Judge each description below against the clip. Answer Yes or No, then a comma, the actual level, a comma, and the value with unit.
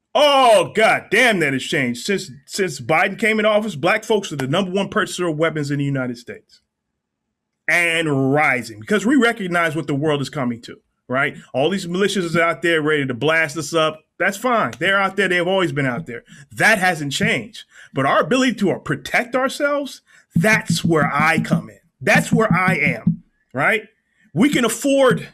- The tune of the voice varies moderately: No, wide, 5.9 semitones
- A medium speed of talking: Yes, average, 190 wpm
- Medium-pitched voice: Yes, medium, 180 Hz